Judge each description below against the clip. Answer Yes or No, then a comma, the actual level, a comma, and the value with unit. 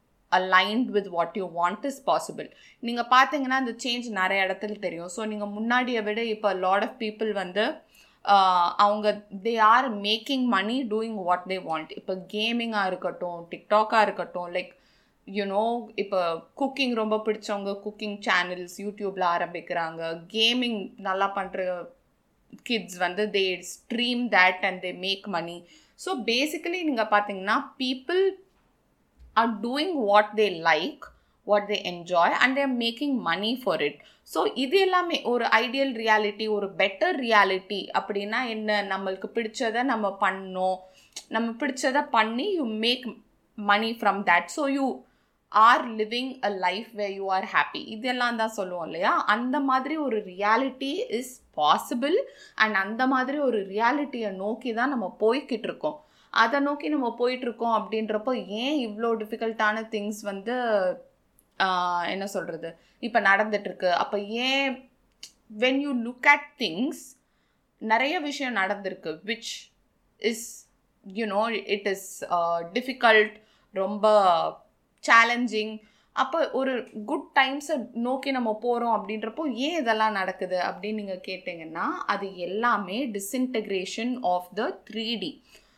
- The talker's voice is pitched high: Yes, high, 220 Hz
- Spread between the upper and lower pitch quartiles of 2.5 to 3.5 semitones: No, average, 4.4 semitones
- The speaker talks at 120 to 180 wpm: Yes, fast, 130 wpm